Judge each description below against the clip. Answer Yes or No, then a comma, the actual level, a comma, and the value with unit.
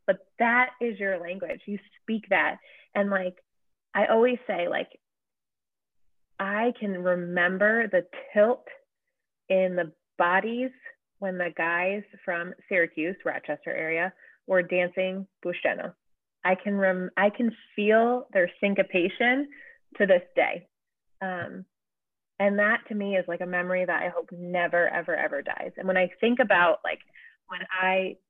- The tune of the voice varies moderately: Yes, average, 4.2 semitones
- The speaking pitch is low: No, high, 195 Hz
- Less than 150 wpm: Yes, average, 140 wpm